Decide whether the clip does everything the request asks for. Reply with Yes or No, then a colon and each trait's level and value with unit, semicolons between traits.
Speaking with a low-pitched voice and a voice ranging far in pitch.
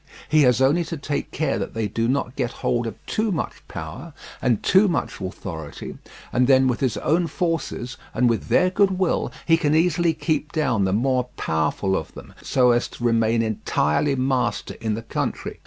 Yes: low, 130 Hz; wide, 5.7 semitones